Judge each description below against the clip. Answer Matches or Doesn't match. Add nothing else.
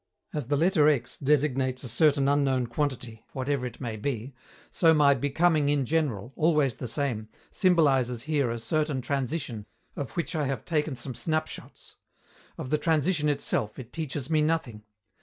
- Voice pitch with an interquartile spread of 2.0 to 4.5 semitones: Matches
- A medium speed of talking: Matches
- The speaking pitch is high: Doesn't match